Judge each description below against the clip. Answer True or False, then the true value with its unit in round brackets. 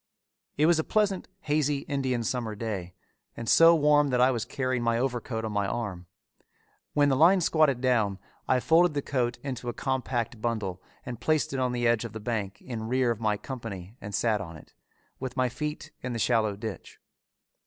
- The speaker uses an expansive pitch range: False (3.8 semitones)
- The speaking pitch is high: False (120 Hz)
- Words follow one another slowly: False (195 wpm)